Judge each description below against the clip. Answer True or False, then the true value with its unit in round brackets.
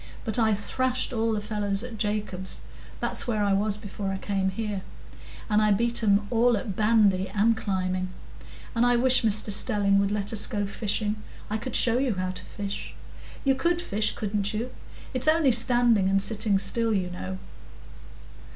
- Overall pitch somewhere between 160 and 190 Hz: False (210 Hz)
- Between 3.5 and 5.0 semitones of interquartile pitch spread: False (2.7 semitones)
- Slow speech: False (175 wpm)